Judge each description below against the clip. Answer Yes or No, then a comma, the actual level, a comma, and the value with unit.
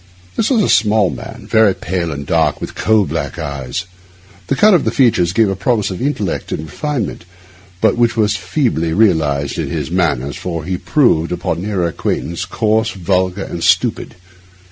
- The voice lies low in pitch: Yes, very low, 95 Hz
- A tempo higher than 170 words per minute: Yes, average, 180 wpm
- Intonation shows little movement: No, average, 5.1 semitones